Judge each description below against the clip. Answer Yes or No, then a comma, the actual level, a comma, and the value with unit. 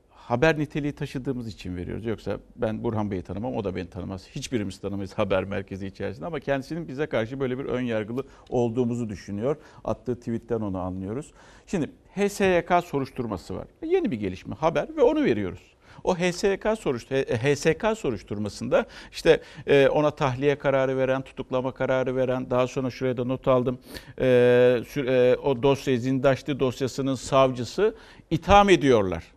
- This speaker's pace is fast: Yes, fast, 145 wpm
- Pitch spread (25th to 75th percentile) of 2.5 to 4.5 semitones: Yes, average, 3.9 semitones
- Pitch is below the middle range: Yes, low, 130 Hz